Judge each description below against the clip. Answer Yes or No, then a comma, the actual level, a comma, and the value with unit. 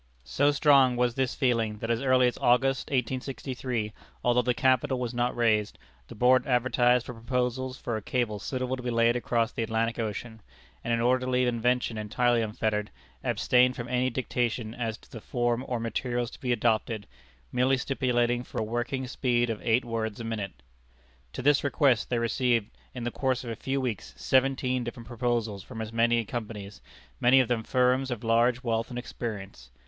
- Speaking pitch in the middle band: No, low, 120 Hz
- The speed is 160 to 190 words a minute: Yes, average, 185 wpm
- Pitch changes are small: Yes, narrow, 1.9 semitones